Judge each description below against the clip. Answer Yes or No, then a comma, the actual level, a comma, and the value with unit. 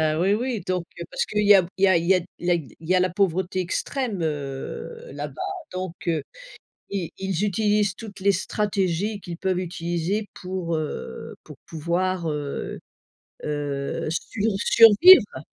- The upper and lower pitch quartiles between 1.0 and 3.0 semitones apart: No, average, 3.4 semitones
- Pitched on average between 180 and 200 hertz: Yes, medium, 185 Hz